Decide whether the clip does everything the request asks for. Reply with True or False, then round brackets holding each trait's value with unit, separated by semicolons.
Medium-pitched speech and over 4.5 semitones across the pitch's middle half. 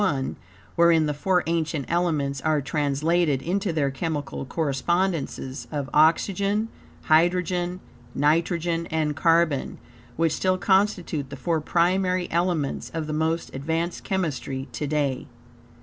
False (165 Hz; 3.2 semitones)